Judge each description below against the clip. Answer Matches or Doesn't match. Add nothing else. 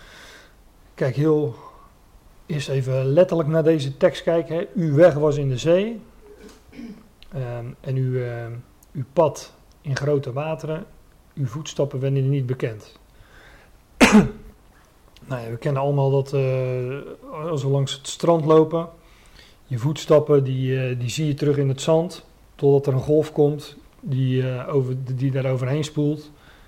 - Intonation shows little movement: Doesn't match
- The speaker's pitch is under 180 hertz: Matches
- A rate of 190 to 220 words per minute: Doesn't match